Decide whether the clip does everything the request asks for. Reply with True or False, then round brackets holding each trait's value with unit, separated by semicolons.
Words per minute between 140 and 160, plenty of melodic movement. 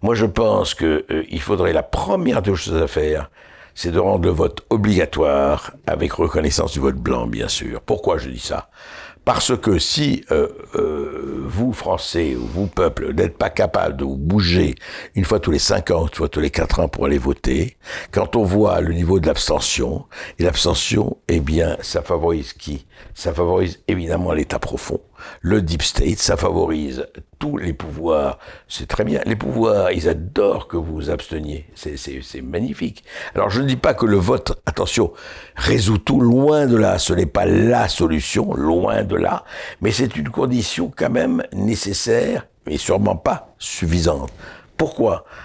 False (180 wpm; 6.2 semitones)